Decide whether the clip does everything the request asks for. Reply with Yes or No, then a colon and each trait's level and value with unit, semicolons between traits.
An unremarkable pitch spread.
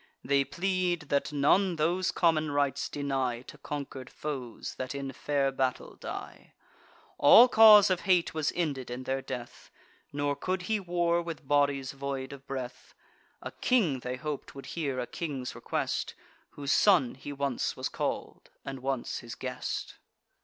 Yes: average, 4.2 semitones